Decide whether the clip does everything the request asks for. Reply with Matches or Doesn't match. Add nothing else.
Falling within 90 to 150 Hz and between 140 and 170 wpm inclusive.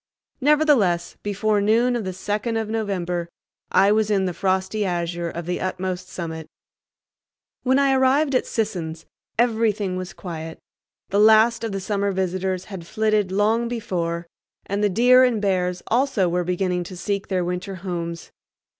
Doesn't match